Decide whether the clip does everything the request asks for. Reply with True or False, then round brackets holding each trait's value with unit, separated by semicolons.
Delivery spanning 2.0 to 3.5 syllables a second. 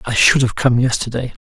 False (5.6 syllables/s)